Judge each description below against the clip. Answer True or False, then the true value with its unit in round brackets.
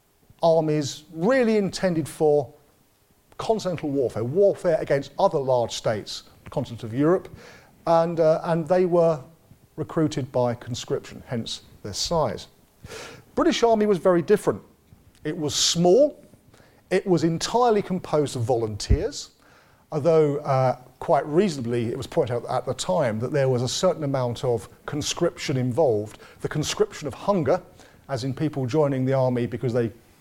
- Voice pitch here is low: False (150 Hz)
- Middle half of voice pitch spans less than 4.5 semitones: False (5.3 semitones)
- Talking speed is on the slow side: False (145 wpm)